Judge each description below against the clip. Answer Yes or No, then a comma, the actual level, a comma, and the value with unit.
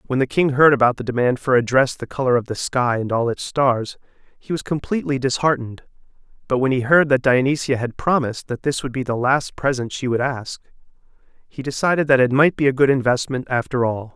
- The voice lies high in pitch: No, low, 130 Hz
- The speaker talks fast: Yes, fast, 220 wpm